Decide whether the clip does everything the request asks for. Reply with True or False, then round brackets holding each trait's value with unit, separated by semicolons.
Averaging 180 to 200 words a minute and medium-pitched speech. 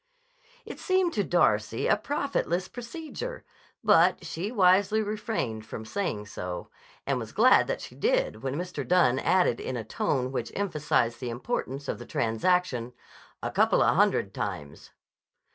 False (145 wpm; 175 Hz)